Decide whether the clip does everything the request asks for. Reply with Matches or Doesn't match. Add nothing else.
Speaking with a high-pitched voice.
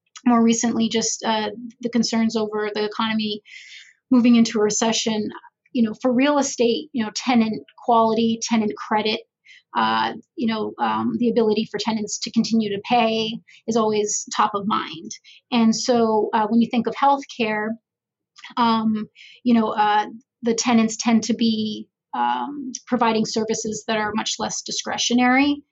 Matches